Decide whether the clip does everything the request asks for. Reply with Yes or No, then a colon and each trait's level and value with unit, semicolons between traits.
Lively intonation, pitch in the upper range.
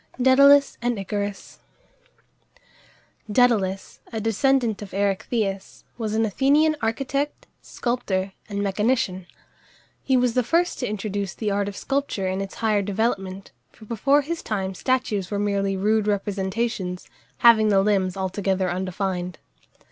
No: average, 3.9 semitones; high, 210 Hz